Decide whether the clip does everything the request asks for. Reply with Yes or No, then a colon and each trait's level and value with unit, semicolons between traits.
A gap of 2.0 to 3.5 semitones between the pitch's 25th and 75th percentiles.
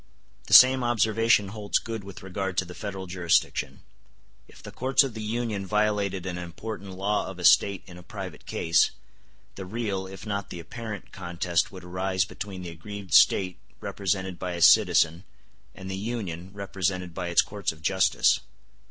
Yes: average, 2.7 semitones